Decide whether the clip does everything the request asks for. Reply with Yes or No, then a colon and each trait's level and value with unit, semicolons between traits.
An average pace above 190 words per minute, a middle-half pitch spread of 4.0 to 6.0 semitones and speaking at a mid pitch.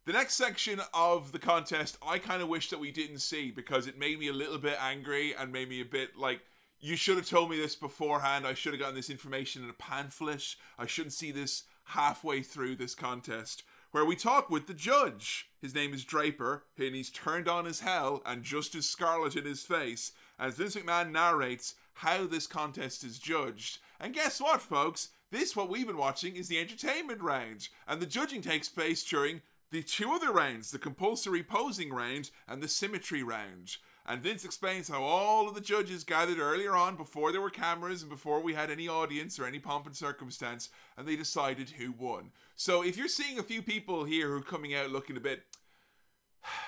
Yes: fast, 205 wpm; average, 4.3 semitones; medium, 155 Hz